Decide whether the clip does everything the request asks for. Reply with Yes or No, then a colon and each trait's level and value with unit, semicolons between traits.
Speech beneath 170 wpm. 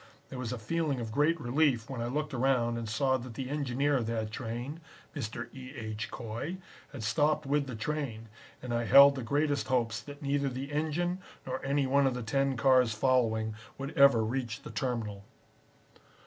No: average, 190 wpm